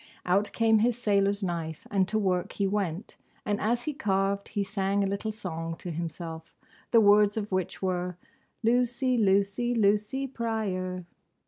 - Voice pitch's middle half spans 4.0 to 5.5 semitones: No, average, 3.0 semitones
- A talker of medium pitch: No, high, 200 Hz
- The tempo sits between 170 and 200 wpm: No, average, 155 wpm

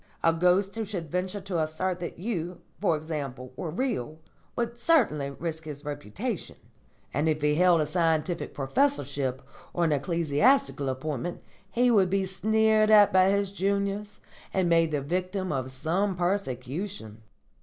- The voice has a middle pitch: Yes, medium, 175 Hz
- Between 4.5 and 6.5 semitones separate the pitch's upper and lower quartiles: Yes, average, 5.0 semitones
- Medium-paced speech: Yes, average, 150 wpm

